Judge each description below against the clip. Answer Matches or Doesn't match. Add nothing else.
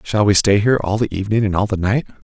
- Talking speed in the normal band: Doesn't match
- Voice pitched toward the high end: Doesn't match